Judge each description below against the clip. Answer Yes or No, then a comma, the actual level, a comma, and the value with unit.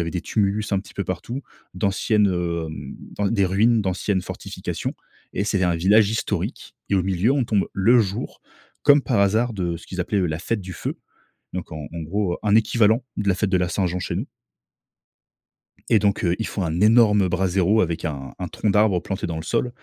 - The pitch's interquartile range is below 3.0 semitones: No, average, 3.3 semitones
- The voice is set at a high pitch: No, very low, 95 Hz